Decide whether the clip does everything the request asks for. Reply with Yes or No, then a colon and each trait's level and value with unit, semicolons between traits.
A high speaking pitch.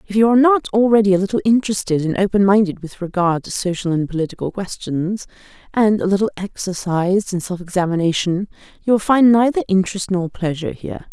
Yes: high, 195 Hz